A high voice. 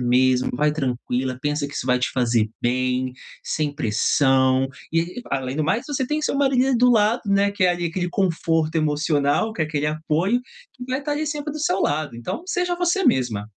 No: medium, 155 Hz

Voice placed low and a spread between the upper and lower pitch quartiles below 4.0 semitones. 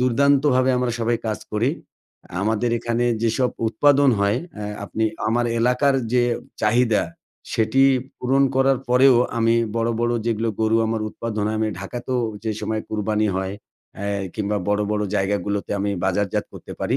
Yes: low, 115 Hz; average, 2.9 semitones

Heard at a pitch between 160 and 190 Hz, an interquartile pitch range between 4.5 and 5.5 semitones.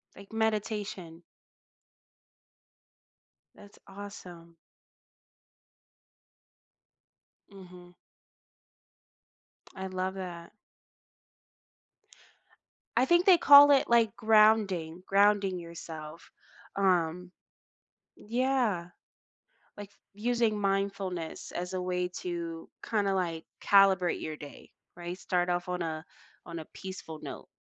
No: medium, 185 Hz; average, 3.1 semitones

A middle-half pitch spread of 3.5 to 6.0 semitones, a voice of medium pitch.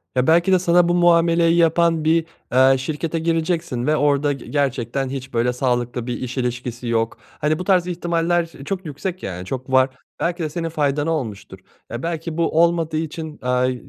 Yes: average, 4.7 semitones; medium, 155 Hz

